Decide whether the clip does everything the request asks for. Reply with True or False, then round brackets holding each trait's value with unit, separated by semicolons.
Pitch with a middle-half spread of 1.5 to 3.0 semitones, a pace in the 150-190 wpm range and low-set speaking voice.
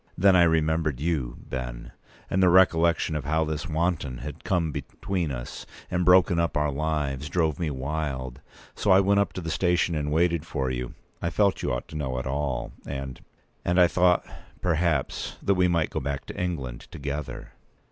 False (4.1 semitones; 185 wpm; 80 Hz)